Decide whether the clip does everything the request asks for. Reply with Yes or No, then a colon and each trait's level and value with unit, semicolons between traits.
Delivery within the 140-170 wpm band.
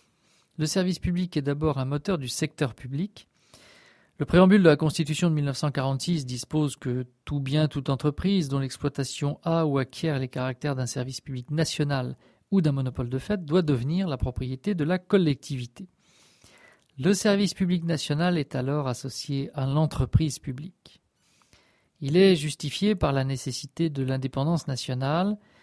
Yes: average, 150 wpm